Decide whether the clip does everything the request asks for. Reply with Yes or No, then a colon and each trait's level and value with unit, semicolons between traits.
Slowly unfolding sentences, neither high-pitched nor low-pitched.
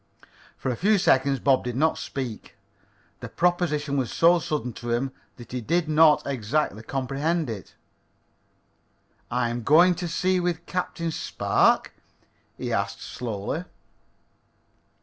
Yes: slow, 130 wpm; medium, 145 Hz